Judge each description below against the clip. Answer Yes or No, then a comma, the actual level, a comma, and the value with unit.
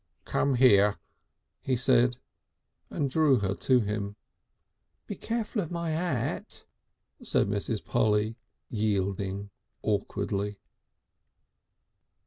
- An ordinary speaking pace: No, slow, 95 wpm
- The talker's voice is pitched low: Yes, low, 110 Hz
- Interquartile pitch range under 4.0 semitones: No, average, 4.8 semitones